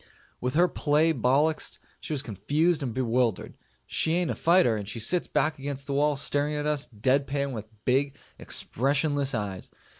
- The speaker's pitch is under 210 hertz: Yes, medium, 140 Hz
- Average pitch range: Yes, average, 3.2 semitones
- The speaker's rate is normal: Yes, average, 175 wpm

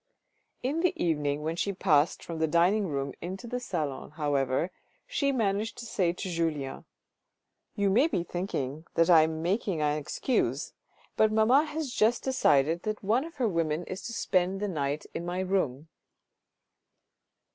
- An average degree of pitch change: No, wide, 5.9 semitones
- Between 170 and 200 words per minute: No, average, 160 wpm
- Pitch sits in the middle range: Yes, medium, 180 Hz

